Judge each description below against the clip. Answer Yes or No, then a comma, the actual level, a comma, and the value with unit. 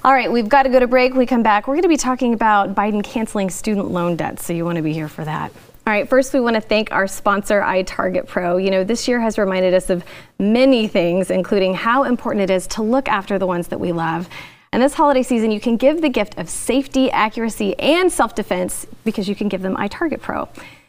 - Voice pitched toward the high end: Yes, high, 215 Hz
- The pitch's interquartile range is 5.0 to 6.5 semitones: Yes, average, 5.3 semitones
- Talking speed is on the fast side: Yes, fast, 250 wpm